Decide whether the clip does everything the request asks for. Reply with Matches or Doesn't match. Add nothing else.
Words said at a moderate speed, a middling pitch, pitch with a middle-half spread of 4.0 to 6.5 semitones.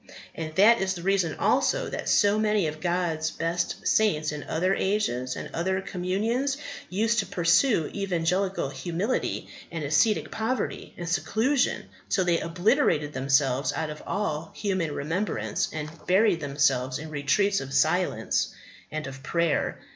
Matches